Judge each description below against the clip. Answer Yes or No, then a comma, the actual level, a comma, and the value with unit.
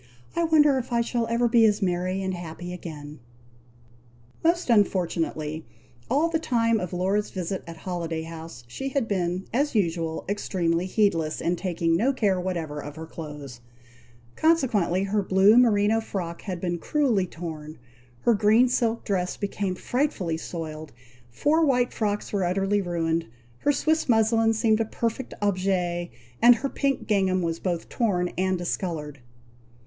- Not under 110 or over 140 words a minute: No, average, 155 wpm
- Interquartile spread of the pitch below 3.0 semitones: No, average, 5.3 semitones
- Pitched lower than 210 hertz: Yes, high, 190 Hz